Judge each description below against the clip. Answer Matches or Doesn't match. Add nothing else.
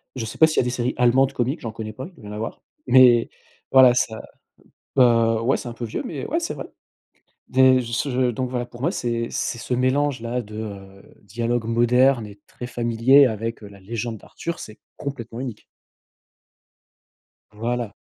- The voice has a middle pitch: Doesn't match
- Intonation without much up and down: Matches